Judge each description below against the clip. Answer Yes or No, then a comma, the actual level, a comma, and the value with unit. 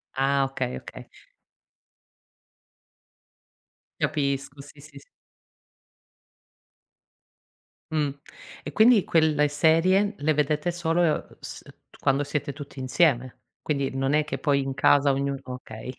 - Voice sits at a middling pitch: Yes, medium, 145 Hz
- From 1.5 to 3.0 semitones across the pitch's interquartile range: Yes, narrow, 2.5 semitones